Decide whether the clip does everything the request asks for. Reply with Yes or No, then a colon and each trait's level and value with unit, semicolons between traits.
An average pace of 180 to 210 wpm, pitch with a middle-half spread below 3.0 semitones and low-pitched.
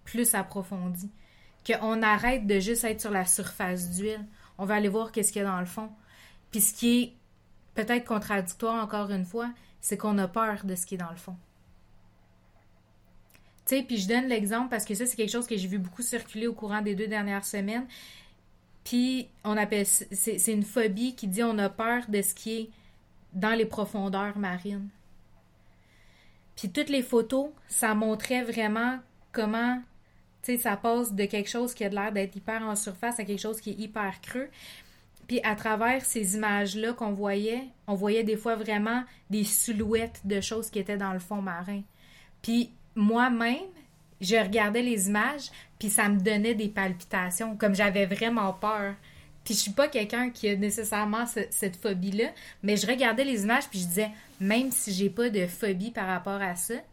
No: average, 190 wpm; narrow, 2.6 semitones; high, 215 Hz